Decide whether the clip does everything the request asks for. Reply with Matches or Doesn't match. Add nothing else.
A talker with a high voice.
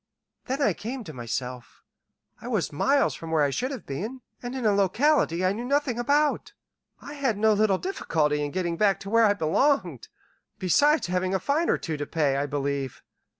Matches